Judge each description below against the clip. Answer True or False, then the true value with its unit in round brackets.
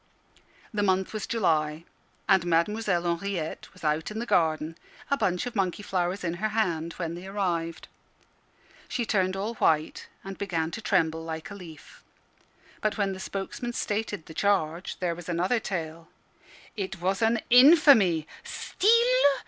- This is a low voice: False (185 Hz)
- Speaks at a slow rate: False (155 wpm)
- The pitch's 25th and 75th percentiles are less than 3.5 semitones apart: False (4.1 semitones)